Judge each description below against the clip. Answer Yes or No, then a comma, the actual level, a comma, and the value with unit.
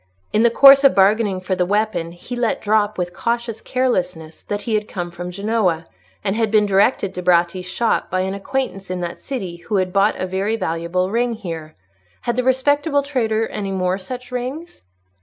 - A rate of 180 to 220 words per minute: Yes, average, 190 wpm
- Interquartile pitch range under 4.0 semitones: No, average, 4.5 semitones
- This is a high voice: Yes, high, 205 Hz